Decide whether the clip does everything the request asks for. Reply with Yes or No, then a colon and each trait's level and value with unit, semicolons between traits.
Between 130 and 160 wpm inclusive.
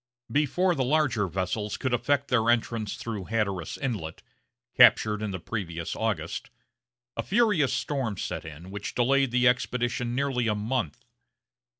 Yes: average, 140 wpm